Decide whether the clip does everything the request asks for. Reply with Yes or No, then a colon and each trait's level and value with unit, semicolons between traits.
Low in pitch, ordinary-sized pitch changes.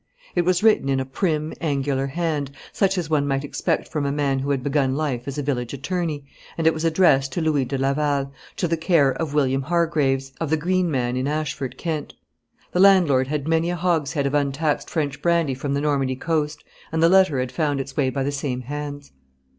No: medium, 145 Hz; average, 3.0 semitones